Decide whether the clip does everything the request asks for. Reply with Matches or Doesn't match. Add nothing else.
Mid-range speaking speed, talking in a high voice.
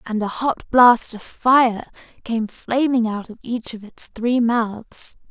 Matches